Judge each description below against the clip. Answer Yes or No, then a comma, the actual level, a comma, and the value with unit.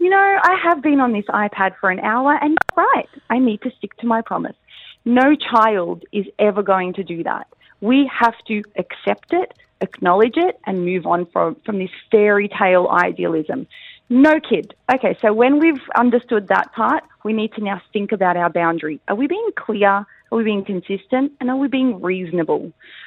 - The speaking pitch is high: Yes, high, 220 Hz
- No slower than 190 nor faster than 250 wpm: Yes, average, 195 wpm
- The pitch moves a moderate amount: No, wide, 5.8 semitones